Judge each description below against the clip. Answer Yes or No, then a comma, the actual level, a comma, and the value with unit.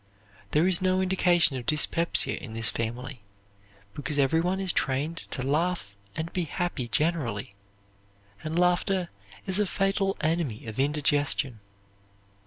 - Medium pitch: Yes, medium, 155 Hz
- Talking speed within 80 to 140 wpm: Yes, slow, 135 wpm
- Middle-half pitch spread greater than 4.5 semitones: Yes, average, 5.1 semitones